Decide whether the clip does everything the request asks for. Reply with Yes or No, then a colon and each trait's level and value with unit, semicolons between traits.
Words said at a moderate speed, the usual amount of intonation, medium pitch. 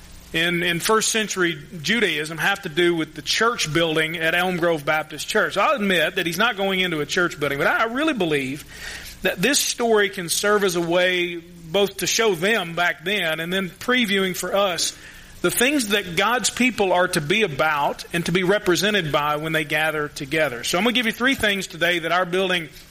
No: fast, 210 wpm; average, 3.8 semitones; medium, 180 Hz